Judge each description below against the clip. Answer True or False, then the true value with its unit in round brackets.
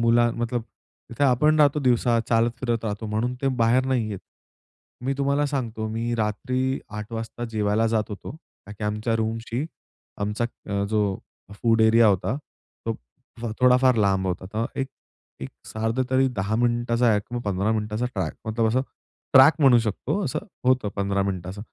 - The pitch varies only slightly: False (3.0 semitones)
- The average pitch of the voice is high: False (115 Hz)